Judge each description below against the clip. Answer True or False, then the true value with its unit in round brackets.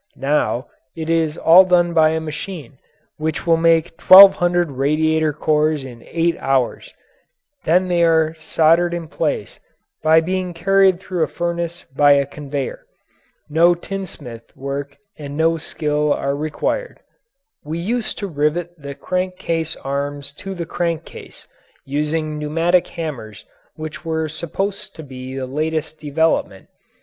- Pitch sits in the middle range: True (160 Hz)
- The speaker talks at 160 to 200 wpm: False (145 wpm)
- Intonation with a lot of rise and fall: False (2.8 semitones)